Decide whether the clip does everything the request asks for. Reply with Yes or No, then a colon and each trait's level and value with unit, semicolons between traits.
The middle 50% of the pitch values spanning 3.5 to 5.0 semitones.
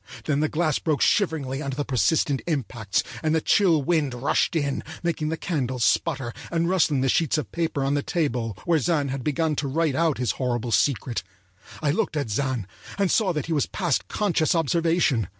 Yes: average, 3.9 semitones